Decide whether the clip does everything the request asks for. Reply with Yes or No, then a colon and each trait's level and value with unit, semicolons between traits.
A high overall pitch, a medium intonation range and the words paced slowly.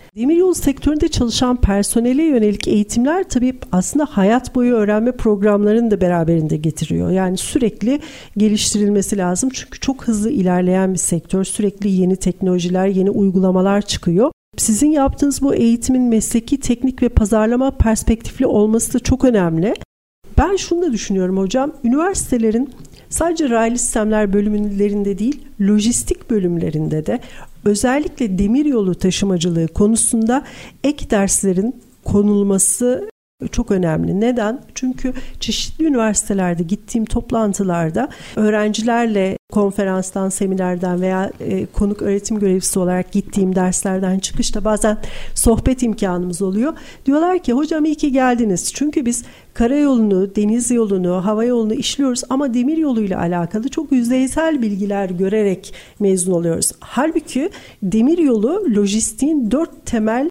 No: high, 220 Hz; average, 4.8 semitones; average, 120 wpm